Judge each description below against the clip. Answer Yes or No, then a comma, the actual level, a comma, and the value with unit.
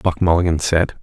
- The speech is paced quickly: No, average, 175 wpm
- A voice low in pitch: Yes, very low, 85 Hz